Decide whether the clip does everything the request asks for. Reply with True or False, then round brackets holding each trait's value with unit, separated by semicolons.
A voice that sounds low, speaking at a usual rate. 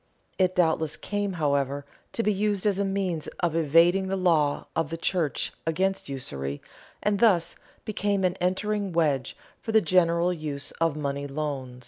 False (170 Hz; 160 wpm)